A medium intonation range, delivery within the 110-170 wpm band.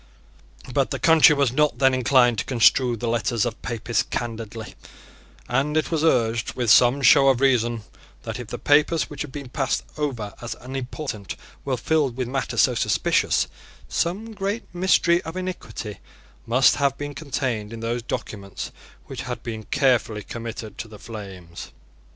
Yes: average, 4.0 semitones; average, 160 wpm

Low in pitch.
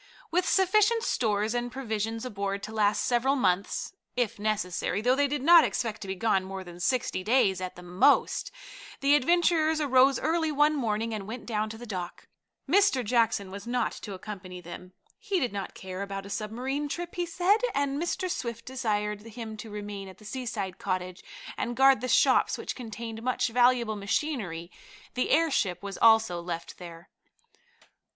No: high, 225 Hz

